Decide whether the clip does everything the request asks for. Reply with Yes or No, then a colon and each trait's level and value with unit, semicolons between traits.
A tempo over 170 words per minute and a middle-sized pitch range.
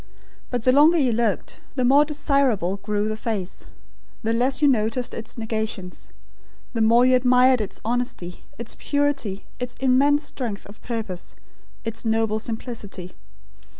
No: average, 145 wpm; average, 3.0 semitones